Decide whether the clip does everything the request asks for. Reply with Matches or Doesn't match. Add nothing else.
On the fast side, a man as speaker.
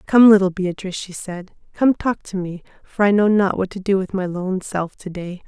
Doesn't match